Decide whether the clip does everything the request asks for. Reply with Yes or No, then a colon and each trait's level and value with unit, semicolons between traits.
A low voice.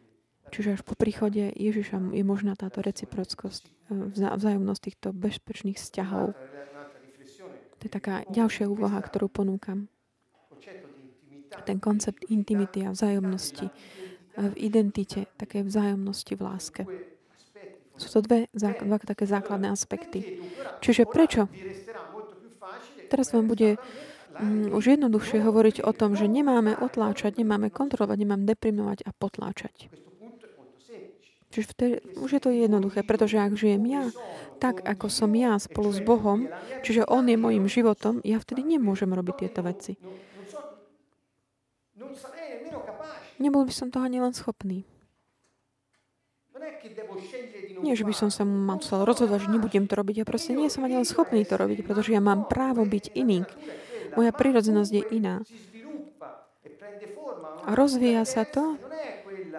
No: high, 210 Hz